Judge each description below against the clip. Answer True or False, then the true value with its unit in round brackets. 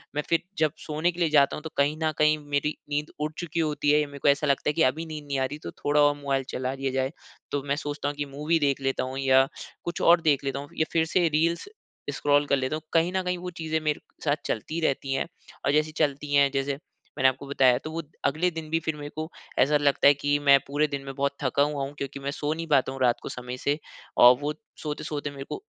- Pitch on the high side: False (145 Hz)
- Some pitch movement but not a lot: False (2.1 semitones)